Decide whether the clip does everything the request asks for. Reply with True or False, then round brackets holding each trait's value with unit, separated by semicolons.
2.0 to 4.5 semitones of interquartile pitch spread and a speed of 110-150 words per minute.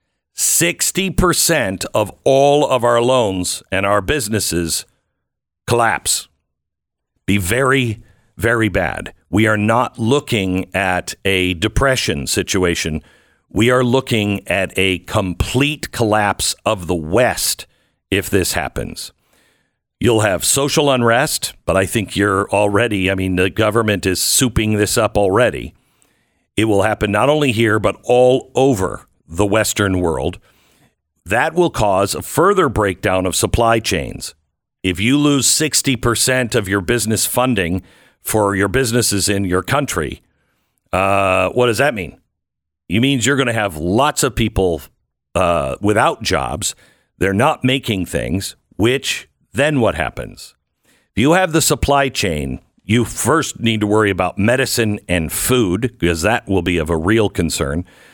False (5.0 semitones; 140 wpm)